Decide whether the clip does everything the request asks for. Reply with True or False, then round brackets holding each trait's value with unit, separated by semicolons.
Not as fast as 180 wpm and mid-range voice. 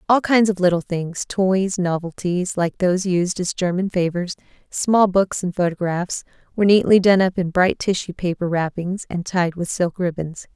True (170 wpm; 180 Hz)